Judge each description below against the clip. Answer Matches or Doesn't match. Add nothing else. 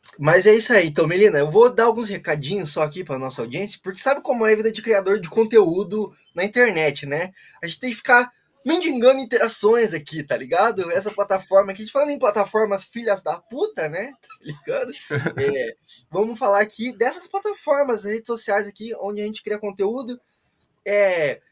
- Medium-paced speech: Doesn't match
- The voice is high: Matches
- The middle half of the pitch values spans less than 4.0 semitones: Doesn't match